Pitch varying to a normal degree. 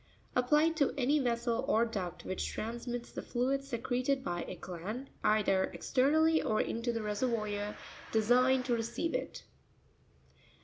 Yes: average, 3.4 semitones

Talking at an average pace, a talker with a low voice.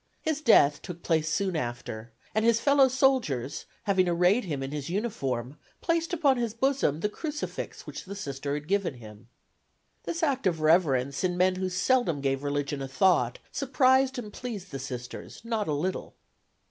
No: average, 170 wpm; medium, 180 Hz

